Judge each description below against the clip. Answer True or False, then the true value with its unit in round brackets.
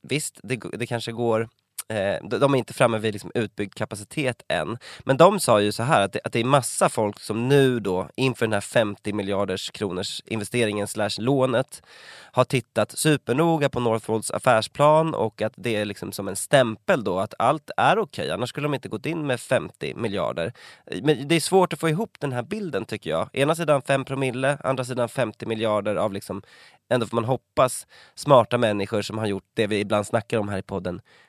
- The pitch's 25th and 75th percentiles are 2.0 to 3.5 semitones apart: False (4.4 semitones)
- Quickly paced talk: True (205 wpm)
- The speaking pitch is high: False (115 Hz)